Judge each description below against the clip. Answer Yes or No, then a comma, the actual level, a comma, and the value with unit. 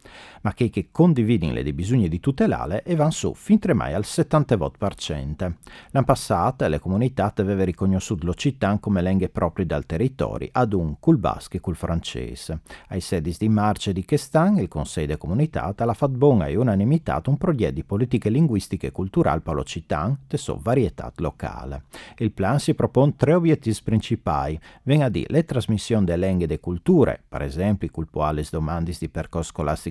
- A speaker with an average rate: No, fast, 175 wpm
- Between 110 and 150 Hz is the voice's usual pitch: No, low, 100 Hz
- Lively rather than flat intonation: Yes, wide, 7.3 semitones